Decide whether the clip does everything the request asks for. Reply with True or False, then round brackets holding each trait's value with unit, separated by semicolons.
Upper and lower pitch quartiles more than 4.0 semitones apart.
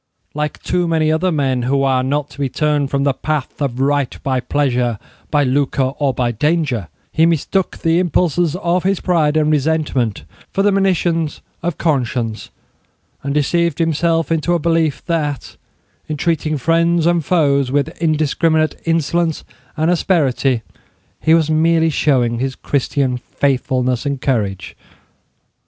False (3.5 semitones)